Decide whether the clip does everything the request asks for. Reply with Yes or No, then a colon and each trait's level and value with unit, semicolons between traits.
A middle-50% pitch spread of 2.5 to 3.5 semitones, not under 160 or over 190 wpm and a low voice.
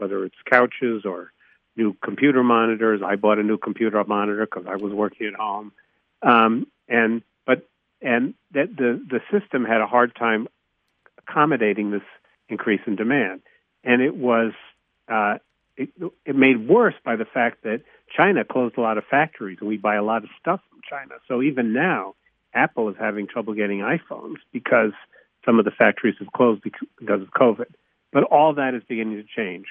Yes: average, 2.9 semitones; average, 180 wpm; low, 115 Hz